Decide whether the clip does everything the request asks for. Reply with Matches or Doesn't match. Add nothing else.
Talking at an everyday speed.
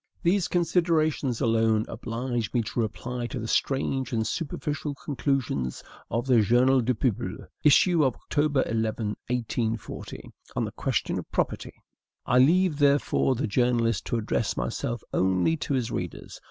Matches